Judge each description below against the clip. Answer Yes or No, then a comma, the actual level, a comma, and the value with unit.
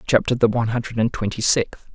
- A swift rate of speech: Yes, fast, 215 wpm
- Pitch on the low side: Yes, low, 115 Hz